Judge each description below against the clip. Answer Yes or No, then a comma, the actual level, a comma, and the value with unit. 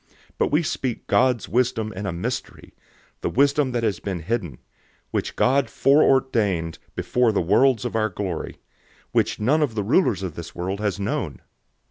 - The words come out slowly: No, average, 175 wpm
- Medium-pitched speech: No, low, 110 Hz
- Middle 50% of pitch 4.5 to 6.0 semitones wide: Yes, average, 5.2 semitones